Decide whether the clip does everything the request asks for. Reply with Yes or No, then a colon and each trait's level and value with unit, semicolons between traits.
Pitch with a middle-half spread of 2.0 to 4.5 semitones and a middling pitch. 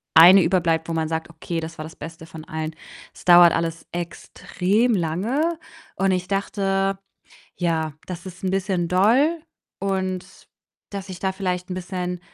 Yes: average, 2.7 semitones; medium, 180 Hz